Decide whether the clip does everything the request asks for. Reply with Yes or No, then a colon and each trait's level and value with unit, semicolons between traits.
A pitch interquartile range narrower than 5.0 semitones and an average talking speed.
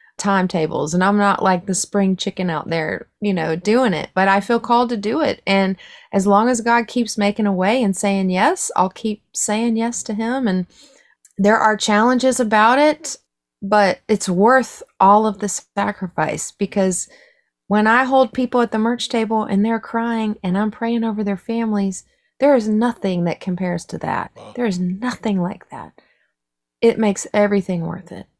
Yes: average, 3.4 semitones; average, 185 wpm